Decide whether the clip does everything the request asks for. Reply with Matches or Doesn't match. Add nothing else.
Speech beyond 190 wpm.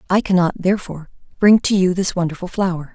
Doesn't match